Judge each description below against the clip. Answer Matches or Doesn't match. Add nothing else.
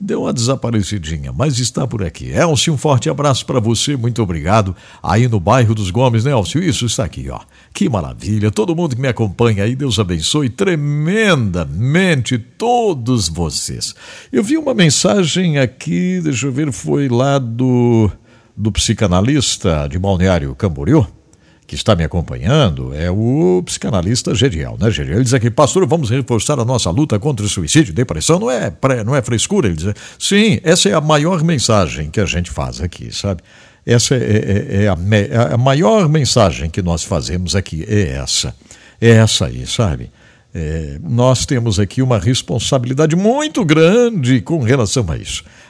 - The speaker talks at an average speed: Matches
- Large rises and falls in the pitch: Matches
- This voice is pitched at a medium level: Doesn't match